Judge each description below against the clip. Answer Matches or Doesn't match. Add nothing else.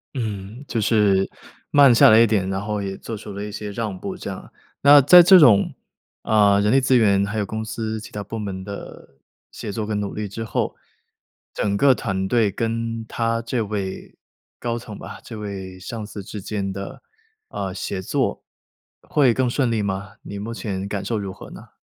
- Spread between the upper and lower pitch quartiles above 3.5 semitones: Doesn't match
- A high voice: Doesn't match